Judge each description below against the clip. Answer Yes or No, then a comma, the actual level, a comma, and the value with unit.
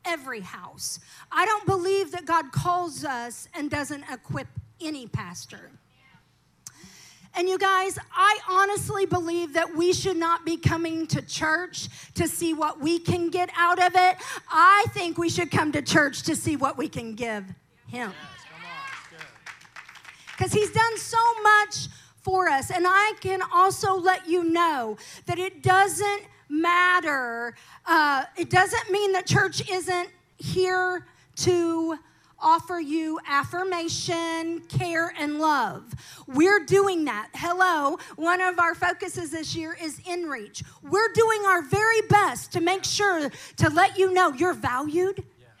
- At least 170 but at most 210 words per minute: No, average, 145 wpm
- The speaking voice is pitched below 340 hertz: No, very high, 350 Hz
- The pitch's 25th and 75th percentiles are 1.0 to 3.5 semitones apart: Yes, average, 2.9 semitones